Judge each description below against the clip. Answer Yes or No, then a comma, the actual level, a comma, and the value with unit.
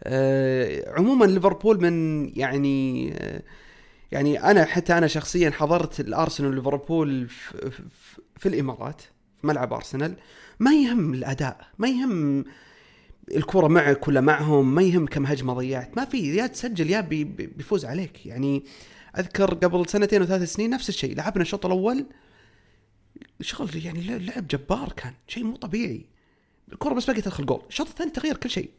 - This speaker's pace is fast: Yes, fast, 150 wpm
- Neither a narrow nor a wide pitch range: No, wide, 6.8 semitones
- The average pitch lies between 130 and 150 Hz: No, medium, 170 Hz